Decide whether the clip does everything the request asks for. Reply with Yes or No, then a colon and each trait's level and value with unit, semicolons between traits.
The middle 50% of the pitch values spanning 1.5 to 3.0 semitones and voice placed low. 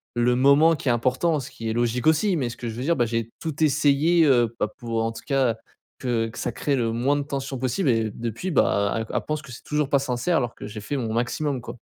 No: average, 3.8 semitones; low, 125 Hz